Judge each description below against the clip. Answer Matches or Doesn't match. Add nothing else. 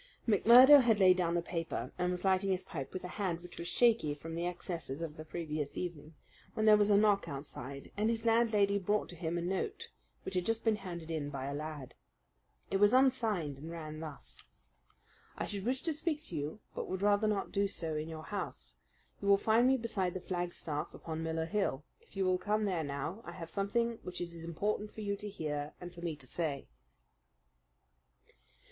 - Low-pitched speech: Doesn't match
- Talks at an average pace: Doesn't match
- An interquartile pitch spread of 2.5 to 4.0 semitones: Doesn't match